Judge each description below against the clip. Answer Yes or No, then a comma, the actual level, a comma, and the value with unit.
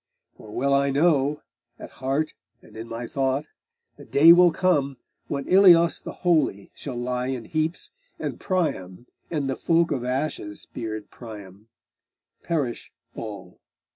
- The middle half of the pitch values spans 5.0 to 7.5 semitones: Yes, average, 5.3 semitones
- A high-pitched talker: No, low, 135 Hz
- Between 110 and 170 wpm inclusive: Yes, average, 140 wpm